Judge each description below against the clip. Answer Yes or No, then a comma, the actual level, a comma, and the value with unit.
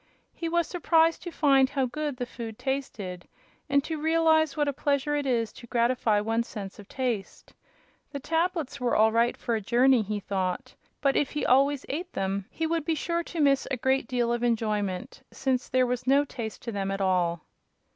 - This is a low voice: No, very high, 255 Hz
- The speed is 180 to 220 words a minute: Yes, average, 200 wpm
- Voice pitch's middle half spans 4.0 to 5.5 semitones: Yes, average, 4.9 semitones